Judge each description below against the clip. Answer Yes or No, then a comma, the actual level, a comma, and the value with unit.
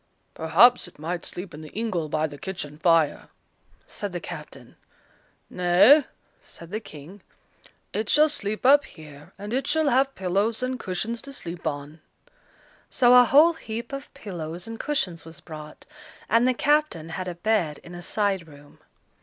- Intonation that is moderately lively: No, wide, 7.0 semitones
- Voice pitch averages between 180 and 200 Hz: Yes, high, 190 Hz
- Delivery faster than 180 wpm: No, average, 165 wpm